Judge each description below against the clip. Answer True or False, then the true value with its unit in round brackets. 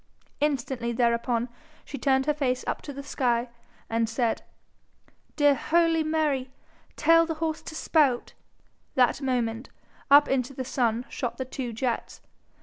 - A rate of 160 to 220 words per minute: False (140 wpm)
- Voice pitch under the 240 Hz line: False (265 Hz)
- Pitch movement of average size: True (3.5 semitones)